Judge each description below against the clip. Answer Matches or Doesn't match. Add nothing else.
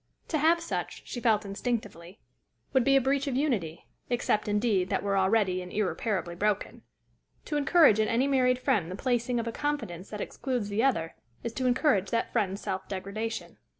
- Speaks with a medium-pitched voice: Doesn't match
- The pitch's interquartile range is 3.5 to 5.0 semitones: Matches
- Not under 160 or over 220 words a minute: Matches